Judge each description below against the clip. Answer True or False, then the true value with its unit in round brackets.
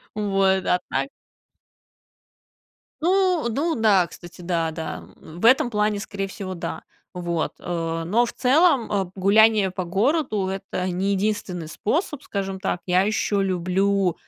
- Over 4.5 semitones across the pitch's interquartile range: False (3.4 semitones)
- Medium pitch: False (195 Hz)